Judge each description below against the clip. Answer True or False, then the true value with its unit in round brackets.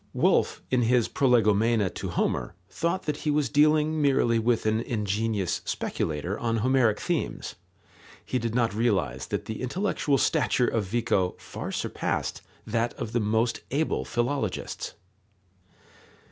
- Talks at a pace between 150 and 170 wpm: False (135 wpm)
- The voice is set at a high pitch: False (115 Hz)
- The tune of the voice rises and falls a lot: False (3.8 semitones)